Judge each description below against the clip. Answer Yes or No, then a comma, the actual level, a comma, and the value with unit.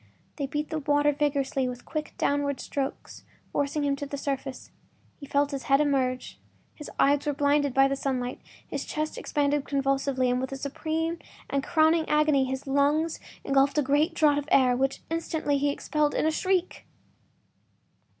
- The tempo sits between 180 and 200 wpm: No, average, 170 wpm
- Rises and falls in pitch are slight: Yes, narrow, 1.7 semitones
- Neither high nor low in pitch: No, very high, 285 Hz